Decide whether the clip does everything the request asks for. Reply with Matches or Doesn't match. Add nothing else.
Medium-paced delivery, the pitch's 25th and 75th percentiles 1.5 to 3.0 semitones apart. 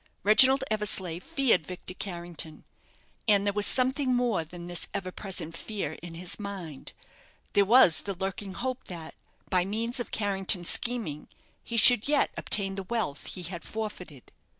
Doesn't match